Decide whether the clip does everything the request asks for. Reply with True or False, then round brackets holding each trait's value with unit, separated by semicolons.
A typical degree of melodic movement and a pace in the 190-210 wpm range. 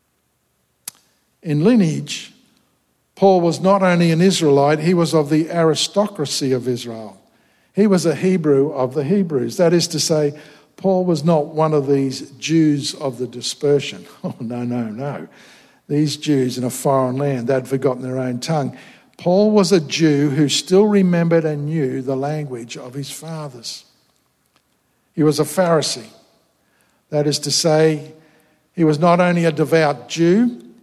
False (3.5 semitones; 155 wpm)